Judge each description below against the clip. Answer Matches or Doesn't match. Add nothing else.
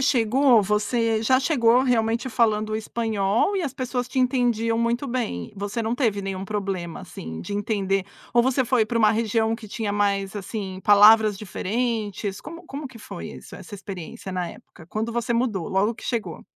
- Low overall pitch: Doesn't match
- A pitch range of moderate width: Matches